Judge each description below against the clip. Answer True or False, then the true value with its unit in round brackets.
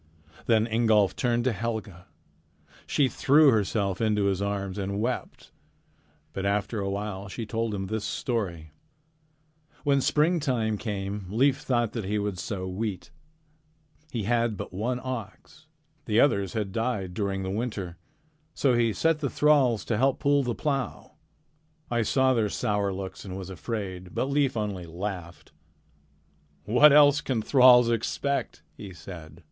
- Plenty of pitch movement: False (4.3 semitones)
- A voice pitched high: False (110 Hz)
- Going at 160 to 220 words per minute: False (150 wpm)